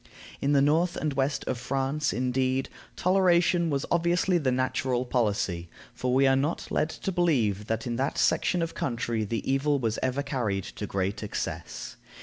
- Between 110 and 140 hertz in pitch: Yes, low, 135 Hz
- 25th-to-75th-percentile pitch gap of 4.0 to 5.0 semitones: Yes, average, 4.5 semitones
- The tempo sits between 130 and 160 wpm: No, average, 170 wpm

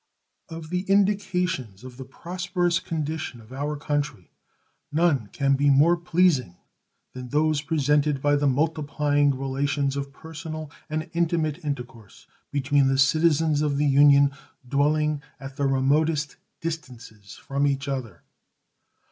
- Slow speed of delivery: Yes, slow, 130 wpm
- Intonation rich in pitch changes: No, narrow, 2.6 semitones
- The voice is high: No, medium, 145 Hz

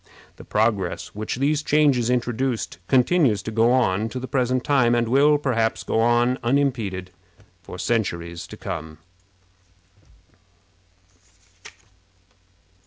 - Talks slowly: Yes, slow, 110 wpm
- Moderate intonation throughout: Yes, average, 3.3 semitones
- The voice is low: Yes, low, 120 Hz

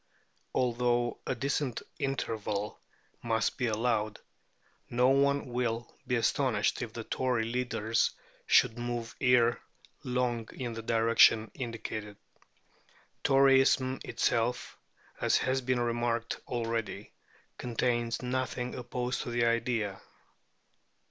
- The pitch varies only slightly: Yes, narrow, 1.7 semitones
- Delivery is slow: Yes, slow, 105 wpm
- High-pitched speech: No, low, 120 Hz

